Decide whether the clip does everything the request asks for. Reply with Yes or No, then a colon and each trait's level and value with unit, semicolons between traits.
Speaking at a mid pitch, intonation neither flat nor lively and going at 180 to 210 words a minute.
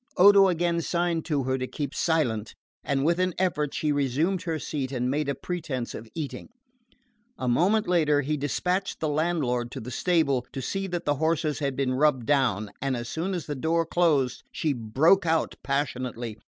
Yes: medium, 150 Hz; average, 4.5 semitones; average, 190 wpm